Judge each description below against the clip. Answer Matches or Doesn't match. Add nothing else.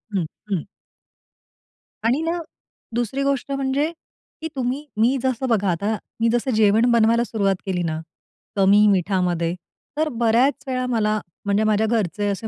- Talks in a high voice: Matches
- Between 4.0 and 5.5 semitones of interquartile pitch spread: Matches